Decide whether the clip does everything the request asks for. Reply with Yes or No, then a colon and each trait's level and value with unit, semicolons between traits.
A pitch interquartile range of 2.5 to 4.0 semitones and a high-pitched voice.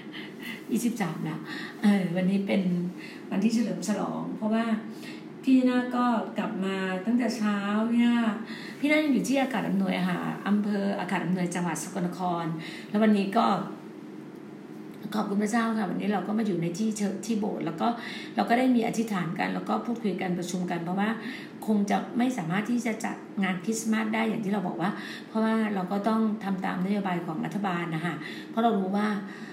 Yes: average, 3.2 semitones; high, 205 Hz